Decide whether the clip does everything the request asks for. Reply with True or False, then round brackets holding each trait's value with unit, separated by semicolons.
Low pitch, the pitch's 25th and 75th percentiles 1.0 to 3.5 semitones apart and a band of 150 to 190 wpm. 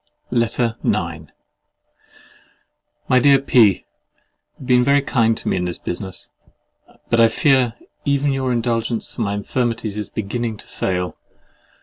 False (115 Hz; 2.9 semitones; 140 wpm)